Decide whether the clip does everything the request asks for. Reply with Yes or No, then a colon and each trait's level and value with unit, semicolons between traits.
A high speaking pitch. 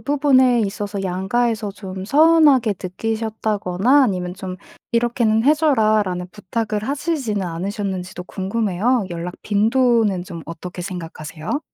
Yes: high, 210 Hz